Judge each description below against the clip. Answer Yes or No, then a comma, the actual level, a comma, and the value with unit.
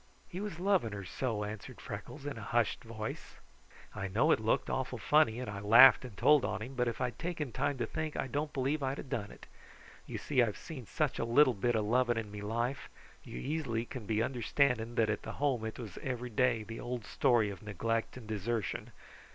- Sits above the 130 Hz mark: No, low, 120 Hz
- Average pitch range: Yes, average, 3.6 semitones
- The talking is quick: Yes, fast, 220 wpm